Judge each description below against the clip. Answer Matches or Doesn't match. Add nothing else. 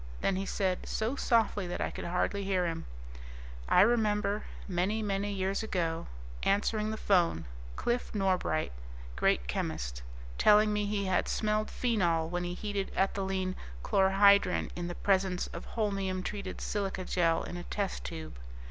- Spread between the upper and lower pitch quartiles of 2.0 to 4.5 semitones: Matches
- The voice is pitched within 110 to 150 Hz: Doesn't match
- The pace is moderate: Matches